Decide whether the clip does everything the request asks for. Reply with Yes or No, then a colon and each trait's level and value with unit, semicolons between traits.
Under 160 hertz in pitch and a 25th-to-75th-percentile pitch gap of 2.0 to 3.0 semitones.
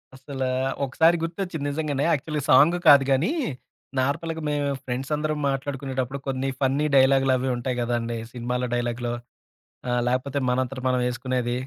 Yes: low, 135 Hz; narrow, 2.4 semitones